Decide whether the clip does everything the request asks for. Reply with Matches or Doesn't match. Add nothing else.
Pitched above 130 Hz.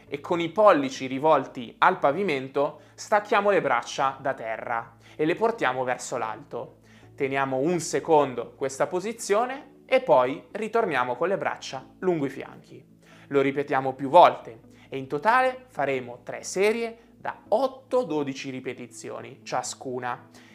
Matches